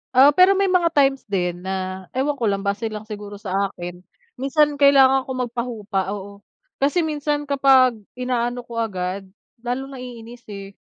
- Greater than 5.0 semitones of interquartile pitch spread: Yes, wide, 5.4 semitones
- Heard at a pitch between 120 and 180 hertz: No, high, 240 Hz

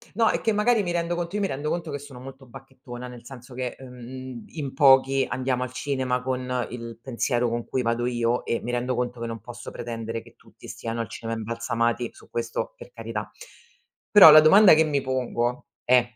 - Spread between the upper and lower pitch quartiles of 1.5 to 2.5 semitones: No, average, 2.9 semitones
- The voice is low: Yes, low, 125 Hz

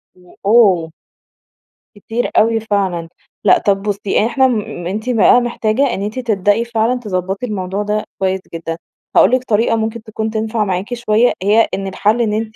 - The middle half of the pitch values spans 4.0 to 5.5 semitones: No, average, 2.8 semitones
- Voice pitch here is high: Yes, high, 215 Hz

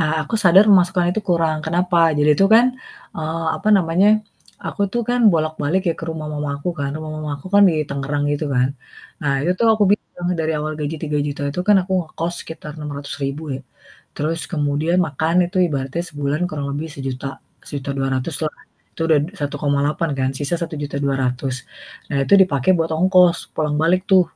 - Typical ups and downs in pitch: Yes, average, 3.4 semitones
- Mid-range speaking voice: Yes, medium, 155 Hz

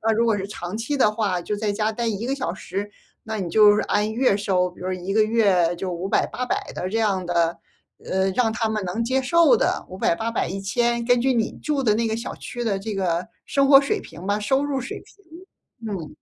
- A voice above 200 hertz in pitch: Yes, high, 215 Hz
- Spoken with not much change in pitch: No, average, 3.8 semitones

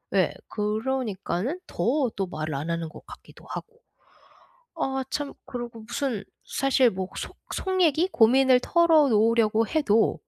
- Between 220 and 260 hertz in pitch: Yes, high, 240 Hz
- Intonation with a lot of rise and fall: No, average, 5.0 semitones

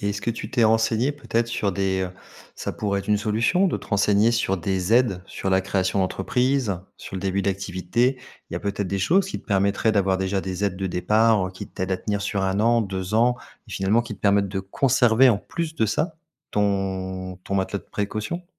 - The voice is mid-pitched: No, low, 100 Hz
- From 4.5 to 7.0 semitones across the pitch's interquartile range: No, average, 3.2 semitones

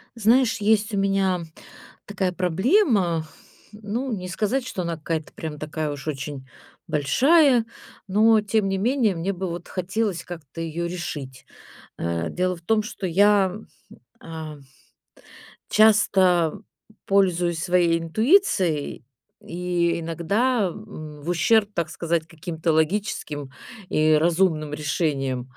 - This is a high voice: No, medium, 180 Hz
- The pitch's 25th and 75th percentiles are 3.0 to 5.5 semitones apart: Yes, average, 4.6 semitones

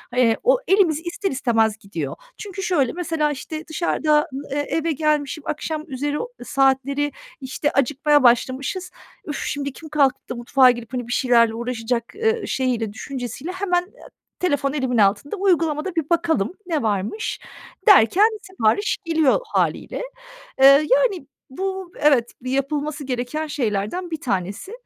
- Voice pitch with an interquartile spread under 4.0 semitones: No, average, 5.3 semitones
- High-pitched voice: Yes, very high, 290 Hz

